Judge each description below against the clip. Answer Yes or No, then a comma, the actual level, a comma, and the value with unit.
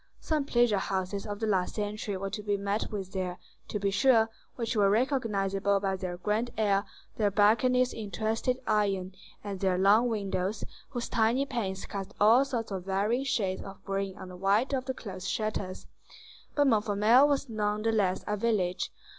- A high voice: Yes, high, 205 Hz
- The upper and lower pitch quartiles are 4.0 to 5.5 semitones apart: No, average, 2.8 semitones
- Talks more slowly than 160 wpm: No, average, 175 wpm